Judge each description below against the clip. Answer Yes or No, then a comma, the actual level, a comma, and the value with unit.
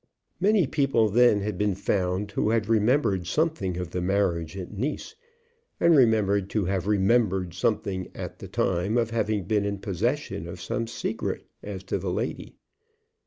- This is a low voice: Yes, low, 100 Hz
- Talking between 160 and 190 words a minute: Yes, average, 165 wpm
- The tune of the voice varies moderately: Yes, average, 3.7 semitones